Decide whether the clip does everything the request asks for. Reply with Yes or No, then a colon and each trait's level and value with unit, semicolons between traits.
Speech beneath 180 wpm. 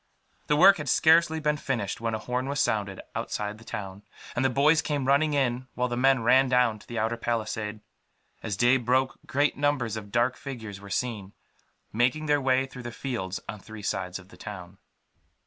No: average, 200 wpm